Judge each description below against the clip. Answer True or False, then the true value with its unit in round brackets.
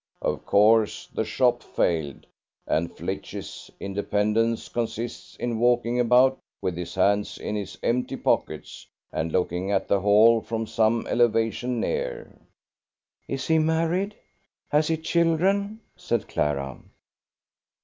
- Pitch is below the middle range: True (115 Hz)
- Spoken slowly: True (120 wpm)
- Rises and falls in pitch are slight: False (4.9 semitones)